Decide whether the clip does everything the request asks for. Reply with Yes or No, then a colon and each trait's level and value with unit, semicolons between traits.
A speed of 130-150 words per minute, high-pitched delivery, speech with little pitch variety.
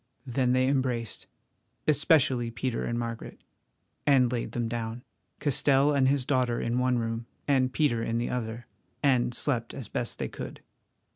No: average, 145 wpm; low, 125 Hz; narrow, 2.3 semitones